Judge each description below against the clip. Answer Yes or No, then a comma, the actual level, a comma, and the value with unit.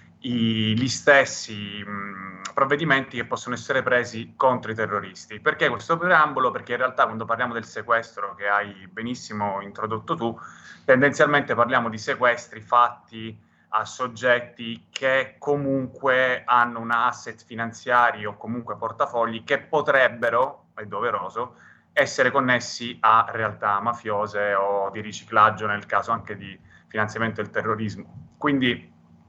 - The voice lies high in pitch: No, low, 115 Hz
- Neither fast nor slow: Yes, average, 125 wpm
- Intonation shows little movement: No, average, 3.0 semitones